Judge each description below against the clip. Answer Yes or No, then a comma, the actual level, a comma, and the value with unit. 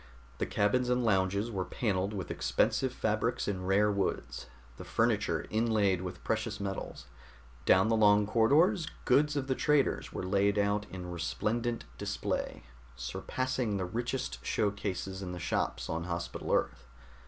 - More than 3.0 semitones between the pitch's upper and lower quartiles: Yes, average, 3.9 semitones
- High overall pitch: No, low, 100 Hz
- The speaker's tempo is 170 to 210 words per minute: No, average, 150 wpm